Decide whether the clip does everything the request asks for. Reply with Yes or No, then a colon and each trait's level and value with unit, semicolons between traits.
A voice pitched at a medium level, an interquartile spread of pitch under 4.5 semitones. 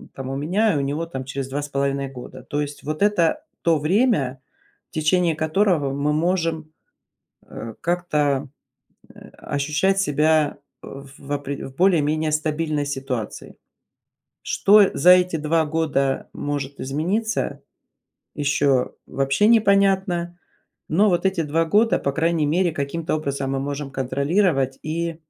Yes: medium, 155 Hz; average, 3.8 semitones